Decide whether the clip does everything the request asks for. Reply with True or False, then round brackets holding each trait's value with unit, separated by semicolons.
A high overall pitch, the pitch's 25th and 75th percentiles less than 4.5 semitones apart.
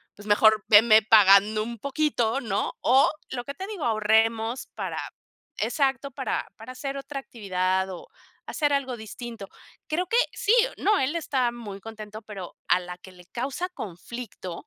False (225 Hz; 4.8 semitones)